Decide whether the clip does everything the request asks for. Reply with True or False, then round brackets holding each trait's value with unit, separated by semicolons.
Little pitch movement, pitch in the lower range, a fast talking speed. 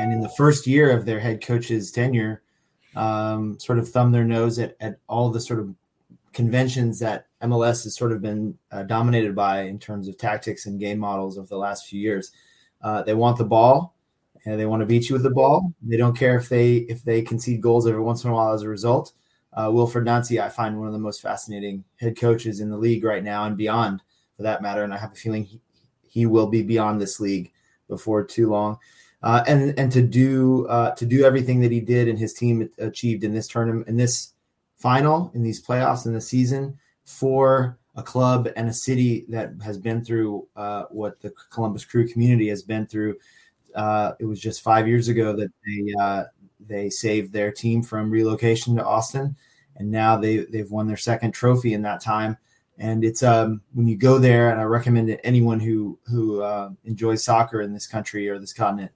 True (2.0 semitones; 115 Hz; 215 wpm)